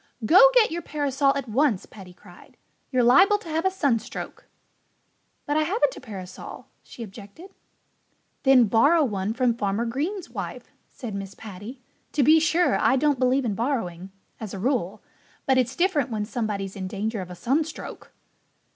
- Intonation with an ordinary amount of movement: No, wide, 6.3 semitones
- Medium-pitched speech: No, very high, 250 Hz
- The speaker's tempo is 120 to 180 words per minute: Yes, average, 165 wpm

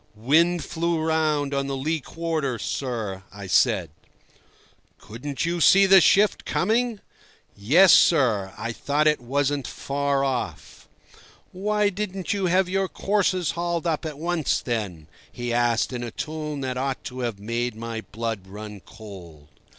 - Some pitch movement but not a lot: No, wide, 6.6 semitones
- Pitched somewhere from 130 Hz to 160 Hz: Yes, medium, 140 Hz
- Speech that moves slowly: No, average, 150 wpm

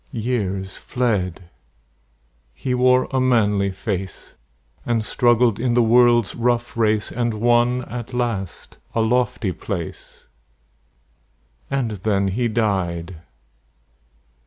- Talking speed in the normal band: No, slow, 105 wpm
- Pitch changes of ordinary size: Yes, average, 3.8 semitones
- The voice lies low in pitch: Yes, low, 115 Hz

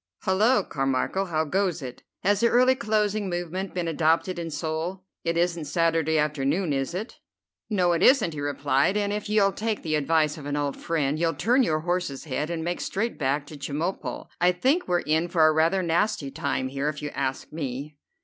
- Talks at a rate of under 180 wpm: No, average, 195 wpm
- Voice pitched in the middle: Yes, medium, 165 Hz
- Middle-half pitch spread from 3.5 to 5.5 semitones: Yes, average, 4.3 semitones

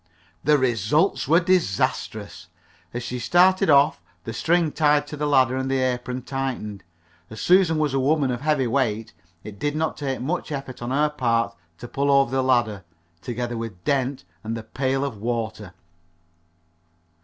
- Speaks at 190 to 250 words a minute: No, average, 165 wpm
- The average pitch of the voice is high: No, low, 130 Hz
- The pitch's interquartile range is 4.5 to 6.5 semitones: No, average, 3.9 semitones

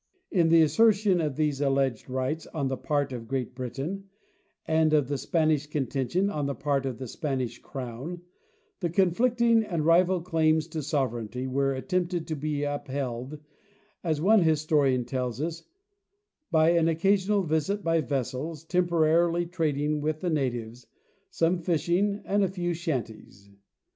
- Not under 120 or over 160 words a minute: Yes, average, 150 wpm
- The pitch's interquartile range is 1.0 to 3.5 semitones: No, average, 4.2 semitones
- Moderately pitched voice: Yes, medium, 155 Hz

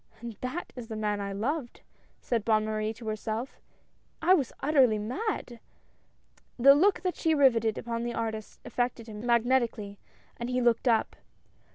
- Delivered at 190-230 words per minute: No, average, 160 wpm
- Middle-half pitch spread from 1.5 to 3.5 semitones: Yes, average, 3.1 semitones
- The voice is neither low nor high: No, high, 235 Hz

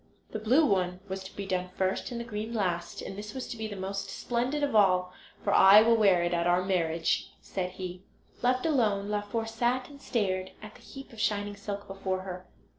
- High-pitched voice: Yes, high, 200 Hz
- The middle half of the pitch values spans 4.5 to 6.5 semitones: No, average, 3.4 semitones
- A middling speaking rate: No, fast, 215 wpm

